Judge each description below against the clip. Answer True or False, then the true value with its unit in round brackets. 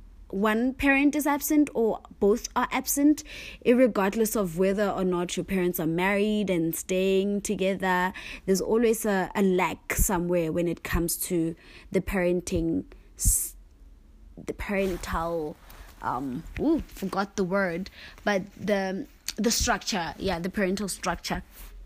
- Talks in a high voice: True (195 Hz)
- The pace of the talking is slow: True (130 wpm)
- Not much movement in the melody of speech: False (3.3 semitones)